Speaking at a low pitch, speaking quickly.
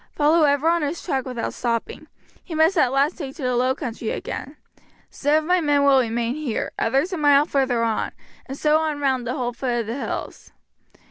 No: very high, 275 Hz; fast, 210 wpm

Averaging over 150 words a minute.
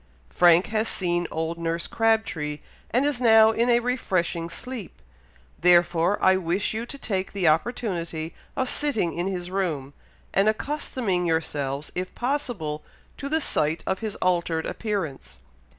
No: average, 145 wpm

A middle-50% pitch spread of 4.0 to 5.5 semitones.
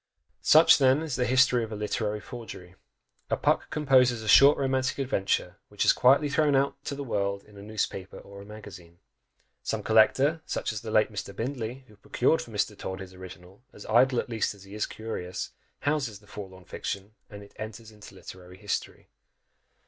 Yes: average, 4.8 semitones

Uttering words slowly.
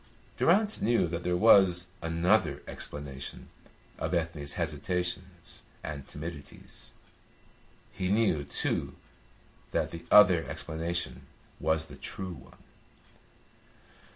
Yes: slow, 95 wpm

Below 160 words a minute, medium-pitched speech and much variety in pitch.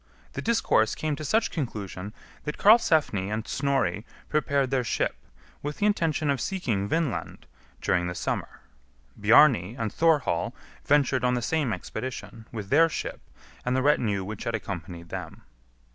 No: average, 150 wpm; low, 125 Hz; wide, 6.4 semitones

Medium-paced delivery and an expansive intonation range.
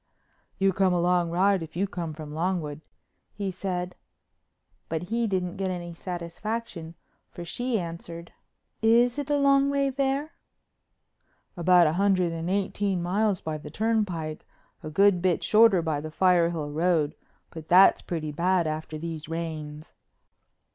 No: average, 145 wpm; average, 3.5 semitones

